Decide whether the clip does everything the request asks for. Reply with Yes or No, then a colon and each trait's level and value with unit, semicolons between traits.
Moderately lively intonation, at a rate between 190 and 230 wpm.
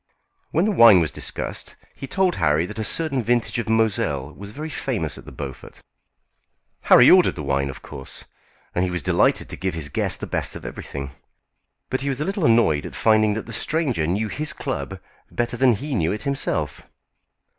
No: wide, 8.7 semitones; average, 195 wpm